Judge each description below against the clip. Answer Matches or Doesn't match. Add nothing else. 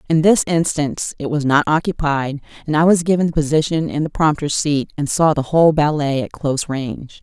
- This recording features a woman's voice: Matches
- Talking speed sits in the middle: Doesn't match